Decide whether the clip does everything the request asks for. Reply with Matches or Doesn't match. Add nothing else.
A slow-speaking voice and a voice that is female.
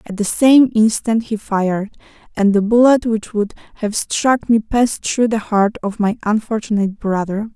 Doesn't match